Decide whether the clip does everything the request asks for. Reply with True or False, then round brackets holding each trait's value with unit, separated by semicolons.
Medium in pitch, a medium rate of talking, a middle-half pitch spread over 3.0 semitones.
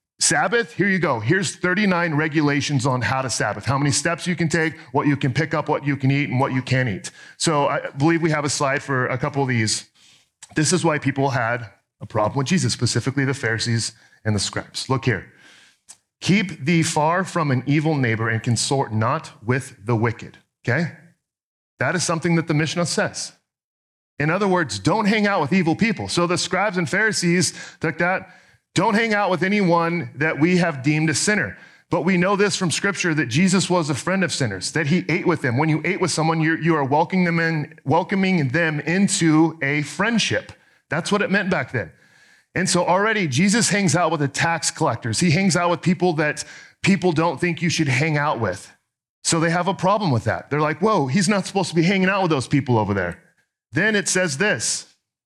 False (160 Hz; 215 wpm; 4.5 semitones)